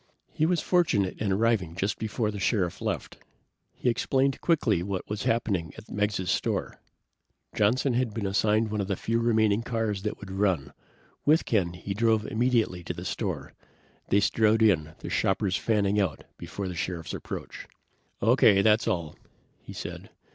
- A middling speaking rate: Yes, average, 165 wpm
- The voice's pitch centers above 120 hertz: No, low, 105 Hz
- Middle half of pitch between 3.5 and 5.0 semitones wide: No, average, 3.0 semitones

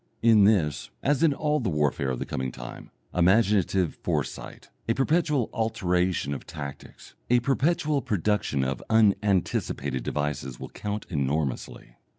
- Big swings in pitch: Yes, wide, 8.0 semitones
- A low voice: Yes, very low, 95 Hz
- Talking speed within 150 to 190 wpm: No, slow, 135 wpm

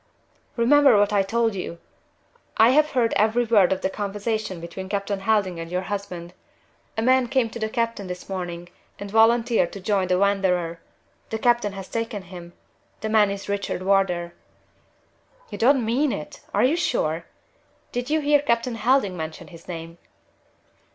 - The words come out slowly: No, average, 165 wpm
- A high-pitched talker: Yes, high, 205 Hz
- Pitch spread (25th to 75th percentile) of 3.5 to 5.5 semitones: Yes, average, 4.1 semitones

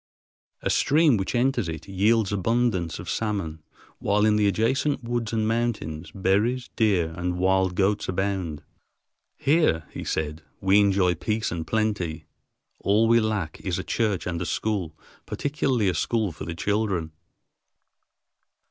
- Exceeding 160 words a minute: No, average, 145 wpm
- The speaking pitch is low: Yes, low, 100 Hz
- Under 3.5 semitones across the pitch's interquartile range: No, average, 4.2 semitones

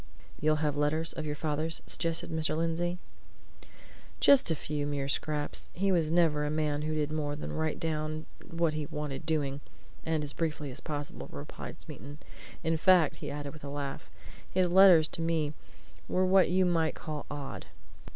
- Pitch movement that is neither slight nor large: No, narrow, 1.9 semitones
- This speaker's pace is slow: No, average, 175 wpm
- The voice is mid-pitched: Yes, medium, 155 Hz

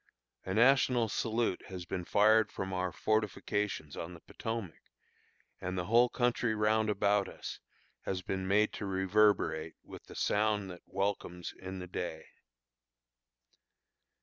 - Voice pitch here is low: Yes, low, 100 Hz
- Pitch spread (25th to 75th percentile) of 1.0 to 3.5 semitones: Yes, average, 2.9 semitones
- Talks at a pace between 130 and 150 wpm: Yes, slow, 135 wpm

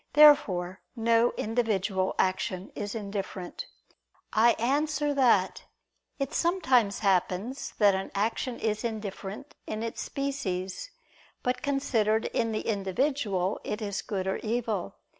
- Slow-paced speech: Yes, slow, 120 wpm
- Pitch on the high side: Yes, high, 220 Hz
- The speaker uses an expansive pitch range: No, average, 4.7 semitones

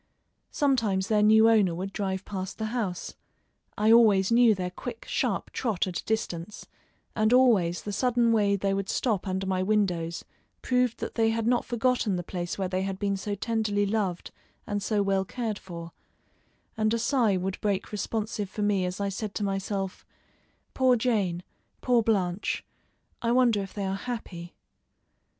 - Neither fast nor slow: Yes, average, 170 wpm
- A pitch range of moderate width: Yes, average, 3.0 semitones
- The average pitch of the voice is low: No, high, 205 Hz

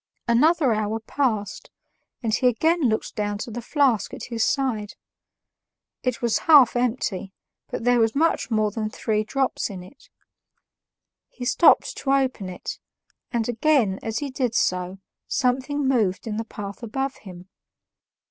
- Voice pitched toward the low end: No, high, 235 Hz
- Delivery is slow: No, average, 150 wpm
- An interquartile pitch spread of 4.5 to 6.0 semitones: No, average, 3.9 semitones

